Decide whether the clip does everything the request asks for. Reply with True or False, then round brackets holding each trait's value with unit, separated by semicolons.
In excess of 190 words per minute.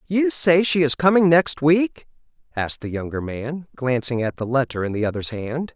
True (200 wpm)